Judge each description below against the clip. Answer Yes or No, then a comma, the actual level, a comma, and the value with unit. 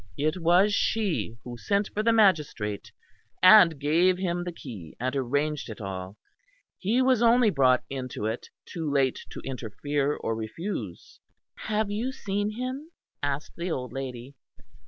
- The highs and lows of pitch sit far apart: Yes, wide, 8.2 semitones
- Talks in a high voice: No, medium, 155 Hz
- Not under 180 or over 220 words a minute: No, average, 150 wpm